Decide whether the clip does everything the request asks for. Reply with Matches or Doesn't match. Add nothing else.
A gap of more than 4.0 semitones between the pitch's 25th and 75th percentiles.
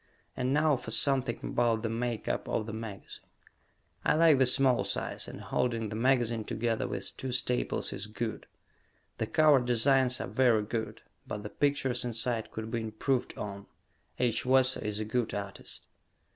Doesn't match